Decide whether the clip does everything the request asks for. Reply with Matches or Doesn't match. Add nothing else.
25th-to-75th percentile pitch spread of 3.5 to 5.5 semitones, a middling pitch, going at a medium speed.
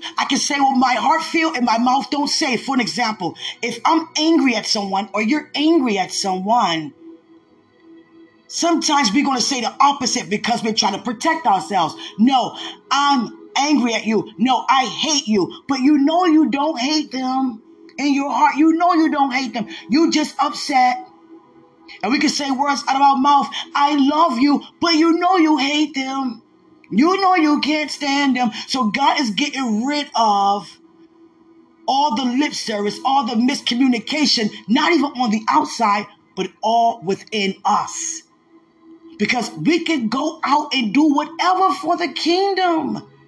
Doesn't match